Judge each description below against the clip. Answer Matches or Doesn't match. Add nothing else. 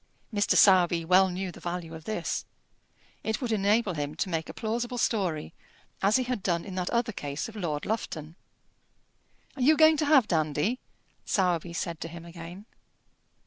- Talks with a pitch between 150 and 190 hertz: Matches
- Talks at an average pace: Matches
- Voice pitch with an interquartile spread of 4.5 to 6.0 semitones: Matches